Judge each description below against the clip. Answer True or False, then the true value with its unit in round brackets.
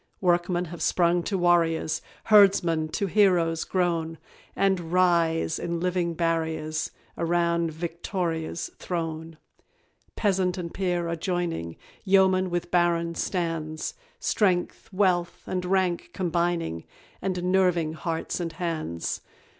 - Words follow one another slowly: True (110 wpm)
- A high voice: False (175 Hz)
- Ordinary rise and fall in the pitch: False (1.8 semitones)